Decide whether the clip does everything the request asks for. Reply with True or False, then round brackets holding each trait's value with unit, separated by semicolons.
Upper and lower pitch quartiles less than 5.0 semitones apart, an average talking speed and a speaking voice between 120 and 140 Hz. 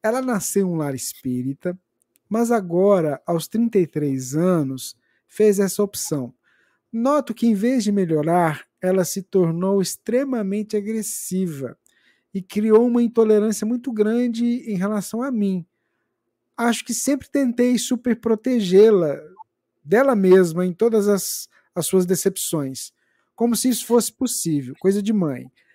False (4.6 semitones; 135 wpm; 205 Hz)